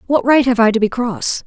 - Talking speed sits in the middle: No, fast, 285 wpm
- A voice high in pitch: Yes, high, 240 Hz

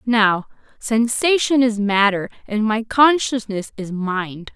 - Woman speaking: Yes, female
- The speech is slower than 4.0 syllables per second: Yes, 3.6 syllables/s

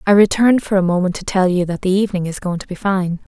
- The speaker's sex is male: No, female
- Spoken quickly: Yes, fast, 285 wpm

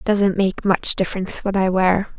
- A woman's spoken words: Yes, female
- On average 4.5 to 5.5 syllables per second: Yes, 5.3 syllables/s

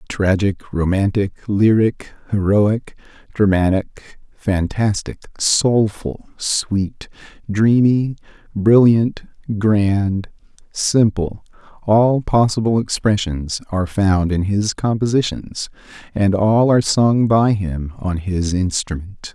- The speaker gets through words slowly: Yes, slow, 90 wpm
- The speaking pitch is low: Yes, low, 105 Hz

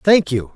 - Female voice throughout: No, male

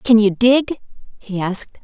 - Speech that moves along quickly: No, average, 165 wpm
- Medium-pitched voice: No, high, 220 Hz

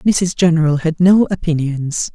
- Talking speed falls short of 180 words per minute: Yes, average, 140 wpm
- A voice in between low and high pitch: Yes, medium, 165 Hz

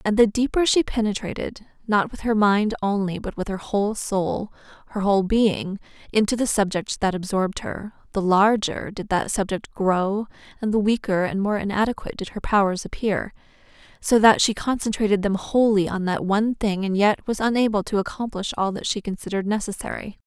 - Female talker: Yes, female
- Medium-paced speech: Yes, average, 180 wpm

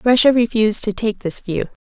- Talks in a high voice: Yes, high, 220 Hz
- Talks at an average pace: Yes, average, 195 wpm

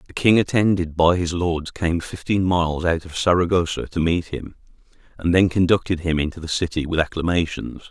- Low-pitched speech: Yes, very low, 85 Hz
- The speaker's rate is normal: Yes, average, 180 wpm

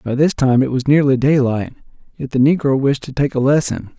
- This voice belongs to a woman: No, male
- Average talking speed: No, fast, 225 wpm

